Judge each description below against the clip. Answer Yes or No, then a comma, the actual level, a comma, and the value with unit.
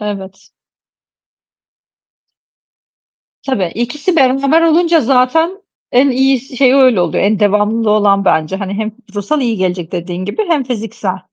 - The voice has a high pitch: Yes, high, 230 Hz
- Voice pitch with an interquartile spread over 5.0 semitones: Yes, wide, 5.4 semitones